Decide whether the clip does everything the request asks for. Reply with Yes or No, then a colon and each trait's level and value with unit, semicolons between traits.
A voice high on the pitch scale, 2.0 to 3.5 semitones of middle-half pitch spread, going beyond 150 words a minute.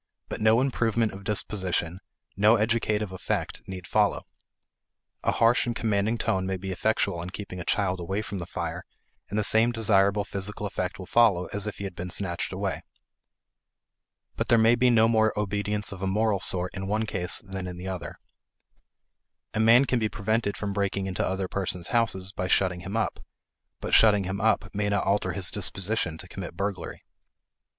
No: low, 100 Hz; narrow, 2.6 semitones; average, 185 wpm